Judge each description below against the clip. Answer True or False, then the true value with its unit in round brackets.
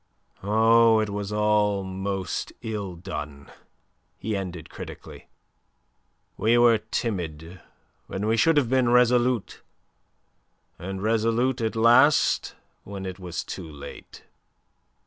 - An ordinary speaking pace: False (110 wpm)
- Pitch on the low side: True (105 Hz)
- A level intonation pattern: False (3.5 semitones)